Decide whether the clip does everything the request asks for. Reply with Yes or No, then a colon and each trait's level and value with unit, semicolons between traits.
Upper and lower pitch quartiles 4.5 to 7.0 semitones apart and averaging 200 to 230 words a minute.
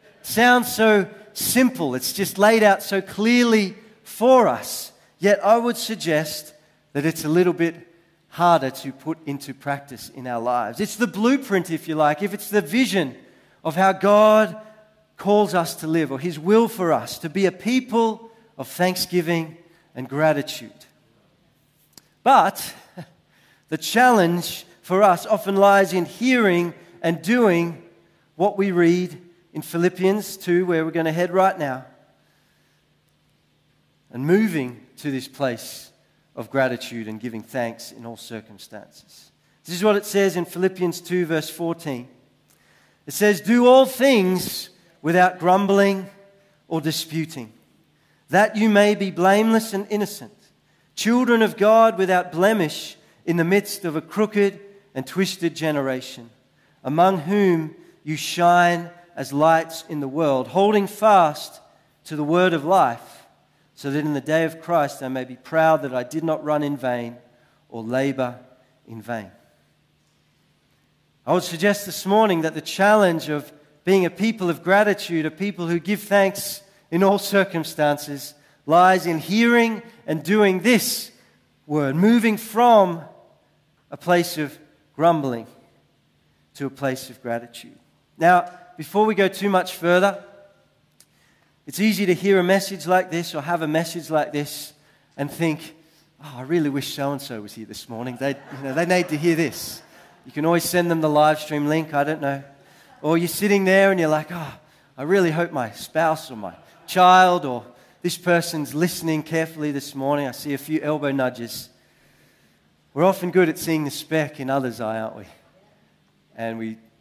No: average, 5.0 semitones; average, 160 wpm